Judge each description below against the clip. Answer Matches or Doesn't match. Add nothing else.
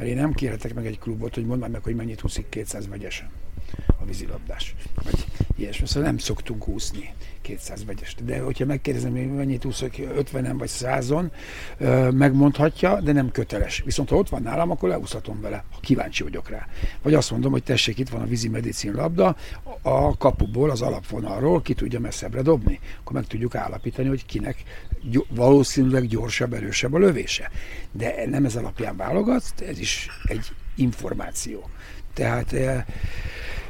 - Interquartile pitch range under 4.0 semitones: Doesn't match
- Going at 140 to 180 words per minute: Matches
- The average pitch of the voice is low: Matches